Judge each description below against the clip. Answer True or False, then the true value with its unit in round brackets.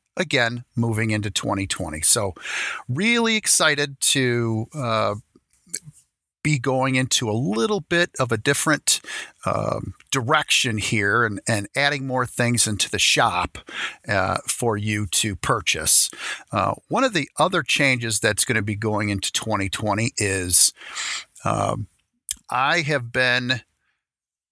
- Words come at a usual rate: False (125 wpm)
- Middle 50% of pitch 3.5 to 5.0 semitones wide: True (4.7 semitones)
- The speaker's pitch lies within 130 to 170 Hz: False (120 Hz)